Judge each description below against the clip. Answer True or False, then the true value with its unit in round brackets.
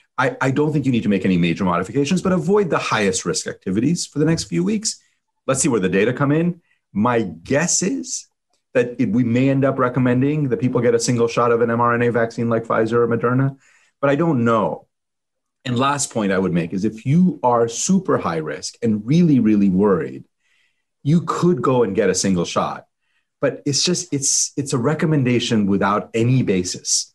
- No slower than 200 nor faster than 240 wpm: True (205 wpm)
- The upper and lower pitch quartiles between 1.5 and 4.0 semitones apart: False (5.2 semitones)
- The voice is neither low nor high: False (130 Hz)